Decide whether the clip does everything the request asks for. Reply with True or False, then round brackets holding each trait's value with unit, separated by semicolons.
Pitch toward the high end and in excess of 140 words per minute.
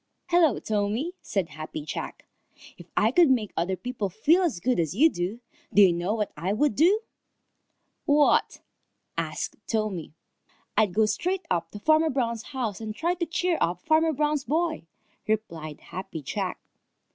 True (220 Hz; 160 wpm)